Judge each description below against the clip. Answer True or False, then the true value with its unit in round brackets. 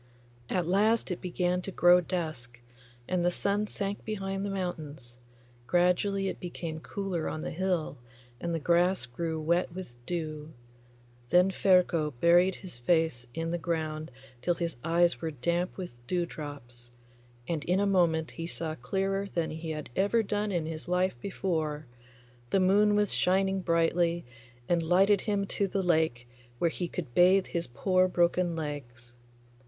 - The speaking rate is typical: True (160 wpm)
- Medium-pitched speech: True (175 Hz)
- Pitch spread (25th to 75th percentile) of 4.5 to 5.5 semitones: False (3.0 semitones)